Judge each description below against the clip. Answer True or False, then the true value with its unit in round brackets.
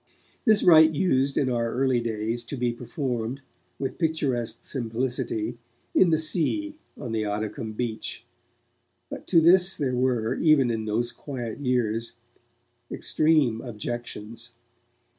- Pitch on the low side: True (125 Hz)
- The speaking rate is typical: False (125 wpm)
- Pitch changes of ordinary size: True (4.7 semitones)